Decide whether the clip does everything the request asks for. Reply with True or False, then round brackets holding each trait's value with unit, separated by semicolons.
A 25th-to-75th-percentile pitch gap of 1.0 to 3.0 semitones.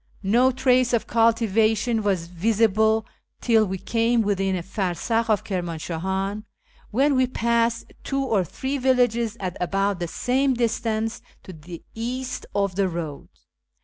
False (3.8 semitones)